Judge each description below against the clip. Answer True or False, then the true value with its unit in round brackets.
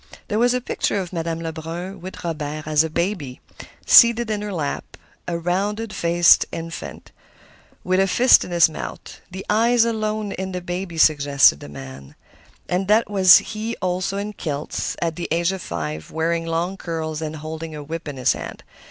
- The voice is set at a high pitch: False (170 Hz)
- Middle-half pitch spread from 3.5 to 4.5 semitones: True (3.9 semitones)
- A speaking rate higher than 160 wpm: True (180 wpm)